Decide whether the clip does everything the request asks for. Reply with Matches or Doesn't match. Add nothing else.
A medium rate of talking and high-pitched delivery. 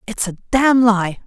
Matches